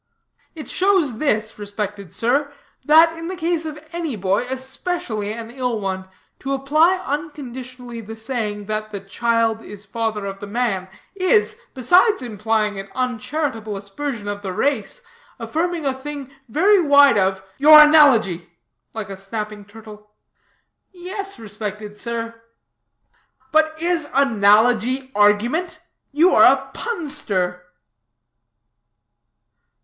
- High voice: Yes, high, 235 Hz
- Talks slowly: Yes, slow, 125 wpm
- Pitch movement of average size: No, wide, 6.4 semitones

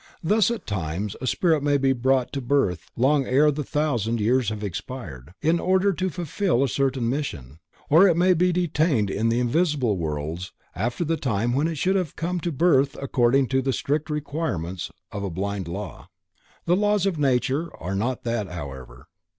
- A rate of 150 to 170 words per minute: No, average, 185 wpm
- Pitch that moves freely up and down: Yes, wide, 7.7 semitones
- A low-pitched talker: Yes, low, 130 Hz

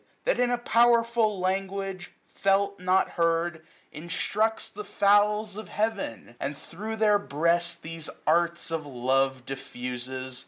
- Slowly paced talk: Yes, slow, 125 wpm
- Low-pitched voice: No, medium, 185 Hz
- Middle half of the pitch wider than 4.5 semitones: Yes, average, 5.2 semitones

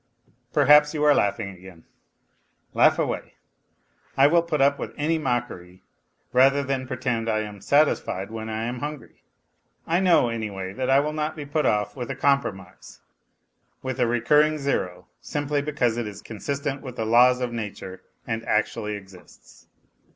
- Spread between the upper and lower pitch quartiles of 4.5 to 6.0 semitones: Yes, average, 5.1 semitones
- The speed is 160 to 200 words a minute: Yes, average, 165 wpm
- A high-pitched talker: No, low, 125 Hz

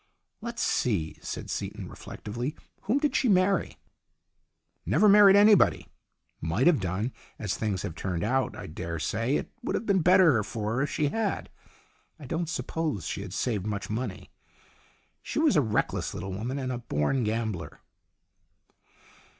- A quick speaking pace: No, average, 160 wpm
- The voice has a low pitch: Yes, low, 125 Hz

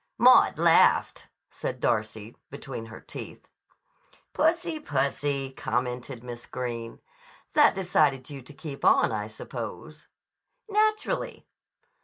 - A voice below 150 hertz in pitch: Yes, low, 135 Hz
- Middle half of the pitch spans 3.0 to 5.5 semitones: Yes, average, 4.6 semitones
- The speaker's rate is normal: No, slow, 105 wpm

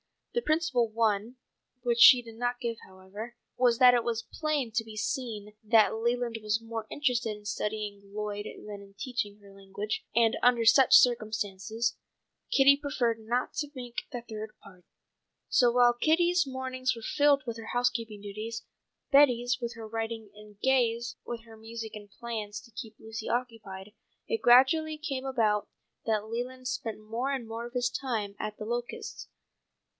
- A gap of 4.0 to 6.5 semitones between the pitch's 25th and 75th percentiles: No, narrow, 2.6 semitones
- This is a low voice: No, high, 230 Hz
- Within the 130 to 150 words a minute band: No, average, 170 wpm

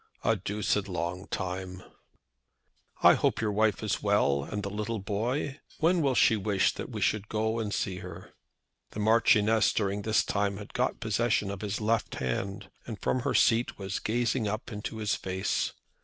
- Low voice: Yes, low, 105 Hz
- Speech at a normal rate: Yes, average, 175 wpm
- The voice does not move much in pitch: Yes, narrow, 2.3 semitones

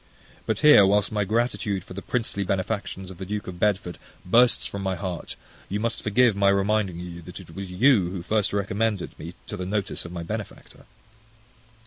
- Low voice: Yes, low, 100 Hz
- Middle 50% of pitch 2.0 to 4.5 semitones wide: Yes, narrow, 2.6 semitones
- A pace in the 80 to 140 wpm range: No, average, 190 wpm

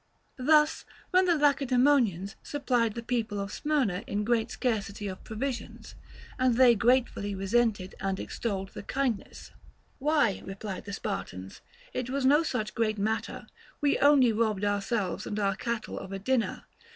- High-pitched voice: Yes, high, 230 Hz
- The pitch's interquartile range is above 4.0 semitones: Yes, average, 4.4 semitones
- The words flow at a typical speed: Yes, average, 150 wpm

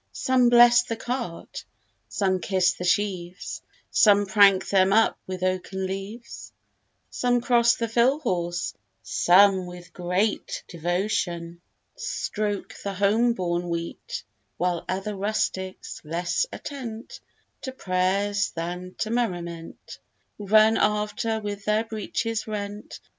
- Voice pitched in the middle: No, high, 200 Hz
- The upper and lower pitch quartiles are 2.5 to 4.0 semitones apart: Yes, average, 3.6 semitones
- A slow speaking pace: Yes, slow, 115 wpm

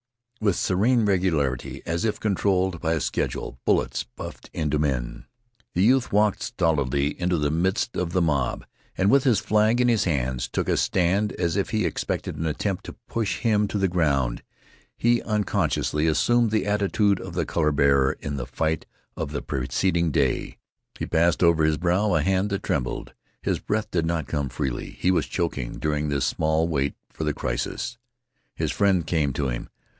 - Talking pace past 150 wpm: Yes, average, 180 wpm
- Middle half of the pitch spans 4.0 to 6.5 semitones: Yes, wide, 5.5 semitones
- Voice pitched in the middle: No, very low, 85 Hz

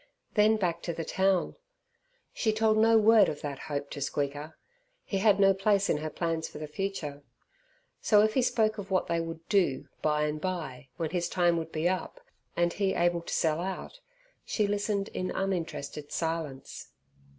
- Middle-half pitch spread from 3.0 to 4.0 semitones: No, average, 4.4 semitones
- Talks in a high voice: No, medium, 175 Hz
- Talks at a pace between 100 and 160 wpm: No, average, 185 wpm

